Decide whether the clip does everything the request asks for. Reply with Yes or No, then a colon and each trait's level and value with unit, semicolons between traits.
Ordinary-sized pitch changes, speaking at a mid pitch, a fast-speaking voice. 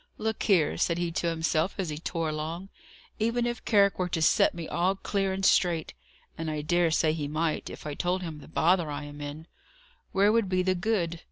Yes: average, 3.3 semitones; medium, 170 Hz; fast, 215 wpm